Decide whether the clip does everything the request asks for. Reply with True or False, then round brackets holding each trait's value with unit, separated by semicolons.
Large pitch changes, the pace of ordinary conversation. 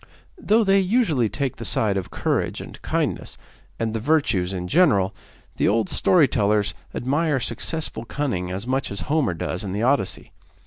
True (7.3 semitones; 170 wpm)